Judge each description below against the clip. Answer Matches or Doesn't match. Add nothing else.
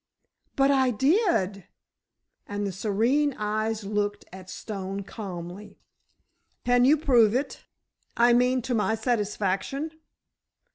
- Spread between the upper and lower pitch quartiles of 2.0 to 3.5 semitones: Doesn't match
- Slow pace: Matches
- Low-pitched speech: Doesn't match